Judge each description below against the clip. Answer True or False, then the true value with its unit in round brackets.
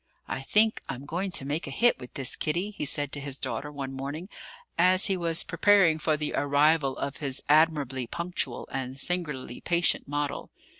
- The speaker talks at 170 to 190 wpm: True (185 wpm)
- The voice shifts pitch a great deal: False (3.9 semitones)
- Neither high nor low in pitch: True (150 Hz)